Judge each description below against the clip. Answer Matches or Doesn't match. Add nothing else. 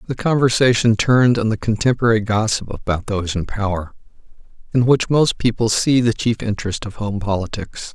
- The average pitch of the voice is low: Matches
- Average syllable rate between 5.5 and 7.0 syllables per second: Matches